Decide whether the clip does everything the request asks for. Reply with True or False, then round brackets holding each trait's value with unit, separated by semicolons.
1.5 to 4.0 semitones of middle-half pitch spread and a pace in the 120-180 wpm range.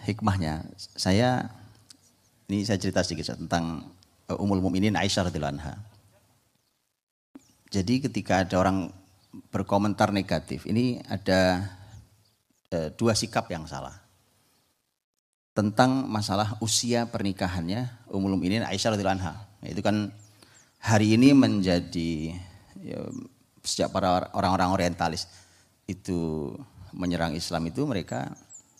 False (2.9 semitones; 95 wpm)